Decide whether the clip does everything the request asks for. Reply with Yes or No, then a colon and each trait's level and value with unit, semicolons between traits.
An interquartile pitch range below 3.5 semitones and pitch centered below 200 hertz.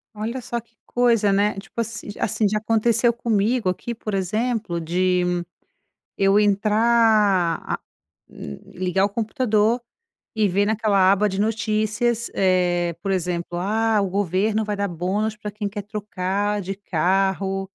No: narrow, 2.5 semitones; high, 205 Hz